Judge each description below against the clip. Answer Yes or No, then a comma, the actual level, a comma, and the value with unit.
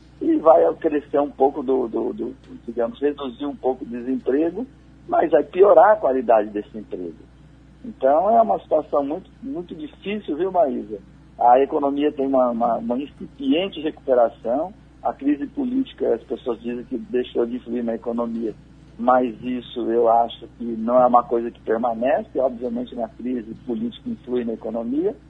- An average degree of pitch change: Yes, average, 4.7 semitones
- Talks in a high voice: No, low, 125 Hz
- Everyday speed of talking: Yes, average, 160 wpm